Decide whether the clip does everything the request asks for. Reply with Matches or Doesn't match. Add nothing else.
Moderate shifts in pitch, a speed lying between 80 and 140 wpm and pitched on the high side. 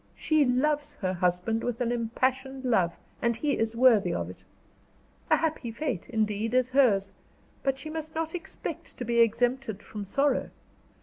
Doesn't match